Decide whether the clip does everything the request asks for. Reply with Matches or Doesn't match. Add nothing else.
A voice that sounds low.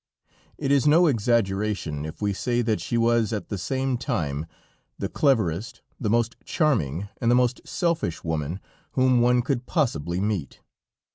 Matches